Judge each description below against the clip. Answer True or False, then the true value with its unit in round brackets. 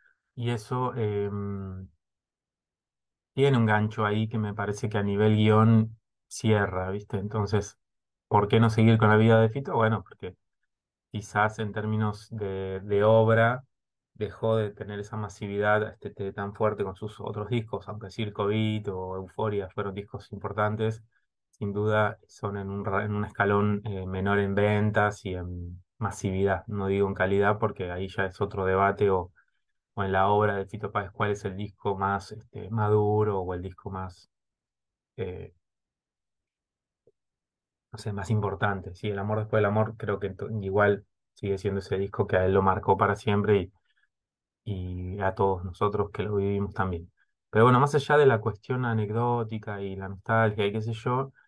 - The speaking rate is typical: True (170 wpm)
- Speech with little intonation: True (1.8 semitones)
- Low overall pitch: True (105 Hz)